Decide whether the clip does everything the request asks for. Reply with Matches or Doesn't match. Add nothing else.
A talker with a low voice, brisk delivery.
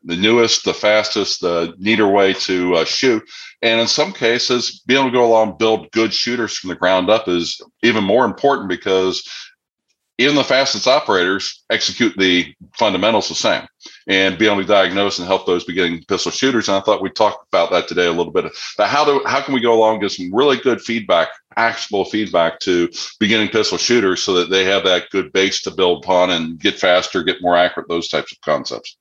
Matches